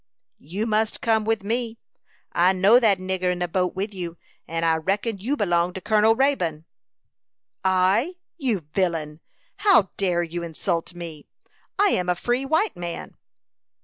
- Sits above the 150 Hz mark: Yes, high, 190 Hz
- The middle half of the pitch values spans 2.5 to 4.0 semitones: No, average, 4.4 semitones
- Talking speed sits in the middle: Yes, average, 155 wpm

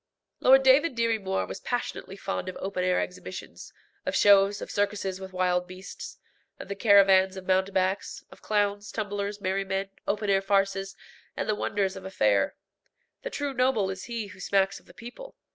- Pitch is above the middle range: Yes, high, 195 Hz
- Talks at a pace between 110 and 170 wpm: No, average, 180 wpm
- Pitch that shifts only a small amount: Yes, narrow, 1.7 semitones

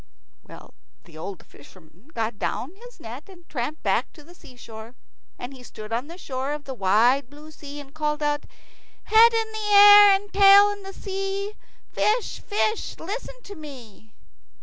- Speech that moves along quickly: No, average, 170 wpm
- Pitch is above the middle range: Yes, very high, 300 Hz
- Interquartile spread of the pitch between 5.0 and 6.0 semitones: No, wide, 8.6 semitones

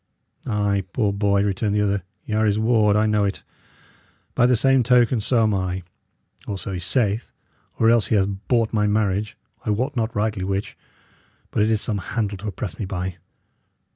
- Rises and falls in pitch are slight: Yes, narrow, 2.0 semitones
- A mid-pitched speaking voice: No, low, 105 Hz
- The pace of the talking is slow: No, average, 195 wpm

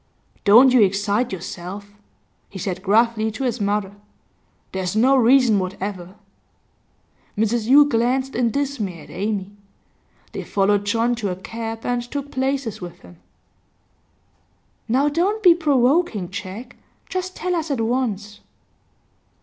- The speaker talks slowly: Yes, slow, 130 wpm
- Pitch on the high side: Yes, high, 225 Hz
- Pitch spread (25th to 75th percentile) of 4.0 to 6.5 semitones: Yes, average, 4.7 semitones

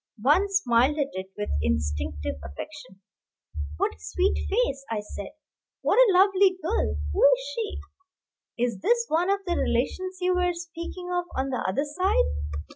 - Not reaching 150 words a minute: No, average, 160 wpm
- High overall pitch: Yes, very high, 300 Hz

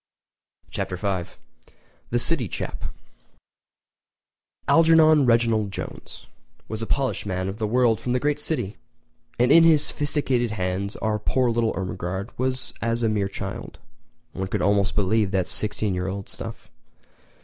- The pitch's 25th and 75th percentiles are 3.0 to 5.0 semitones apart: Yes, average, 4.5 semitones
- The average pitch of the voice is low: Yes, low, 110 Hz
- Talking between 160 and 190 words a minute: No, average, 145 wpm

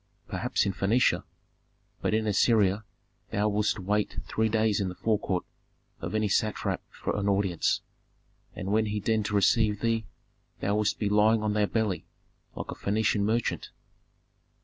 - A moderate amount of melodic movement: No, narrow, 1.5 semitones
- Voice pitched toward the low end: Yes, low, 105 Hz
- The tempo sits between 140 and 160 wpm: Yes, average, 155 wpm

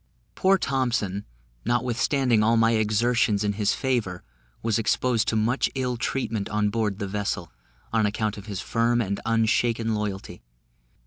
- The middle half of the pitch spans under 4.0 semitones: Yes, narrow, 2.6 semitones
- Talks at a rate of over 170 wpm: No, average, 145 wpm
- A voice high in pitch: No, low, 110 Hz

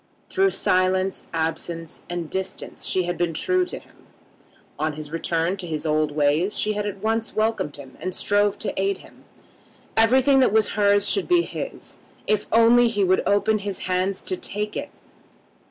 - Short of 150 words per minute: No, average, 175 wpm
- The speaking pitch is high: Yes, high, 195 Hz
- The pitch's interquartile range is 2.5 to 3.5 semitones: No, average, 4.3 semitones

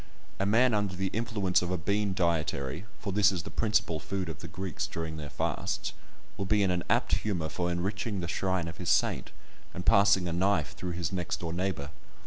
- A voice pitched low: Yes, very low, 90 Hz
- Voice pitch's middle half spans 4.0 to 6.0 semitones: No, average, 3.0 semitones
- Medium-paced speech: No, fast, 210 wpm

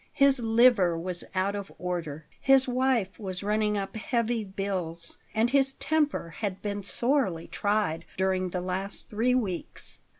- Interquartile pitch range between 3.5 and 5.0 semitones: Yes, average, 4.6 semitones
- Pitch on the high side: Yes, high, 200 Hz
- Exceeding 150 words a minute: No, average, 145 wpm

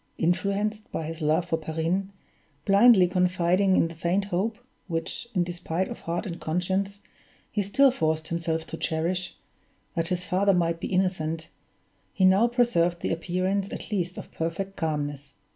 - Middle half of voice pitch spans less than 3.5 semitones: Yes, average, 3.1 semitones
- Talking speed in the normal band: Yes, average, 160 wpm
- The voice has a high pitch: No, medium, 180 Hz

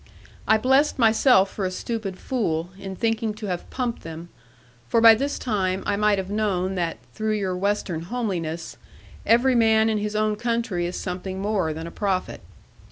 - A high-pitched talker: Yes, high, 205 Hz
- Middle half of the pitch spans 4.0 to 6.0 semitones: No, average, 3.4 semitones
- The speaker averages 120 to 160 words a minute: No, average, 175 wpm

